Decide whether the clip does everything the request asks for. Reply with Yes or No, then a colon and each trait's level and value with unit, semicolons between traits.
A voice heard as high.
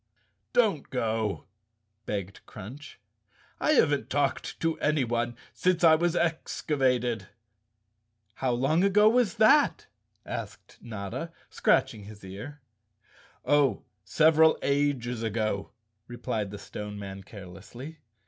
No: low, 125 Hz